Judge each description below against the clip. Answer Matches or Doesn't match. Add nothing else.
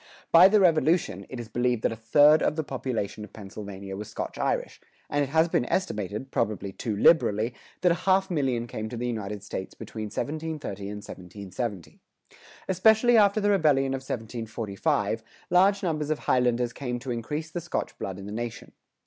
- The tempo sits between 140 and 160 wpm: Doesn't match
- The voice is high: Doesn't match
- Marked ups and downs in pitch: Matches